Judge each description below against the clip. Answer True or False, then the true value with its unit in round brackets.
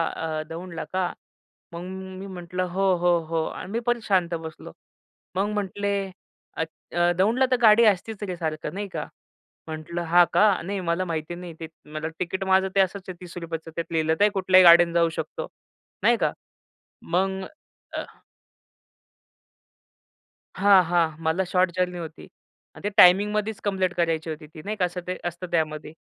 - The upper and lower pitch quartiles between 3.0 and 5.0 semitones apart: False (2.6 semitones)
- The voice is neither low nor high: True (180 Hz)